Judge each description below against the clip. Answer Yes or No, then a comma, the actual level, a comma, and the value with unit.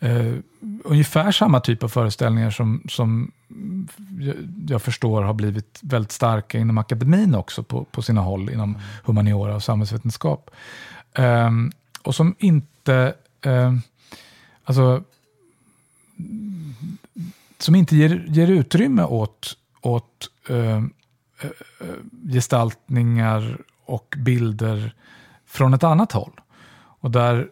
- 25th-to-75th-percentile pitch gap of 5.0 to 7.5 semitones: Yes, wide, 5.5 semitones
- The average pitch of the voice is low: Yes, low, 125 Hz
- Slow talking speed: Yes, slow, 110 wpm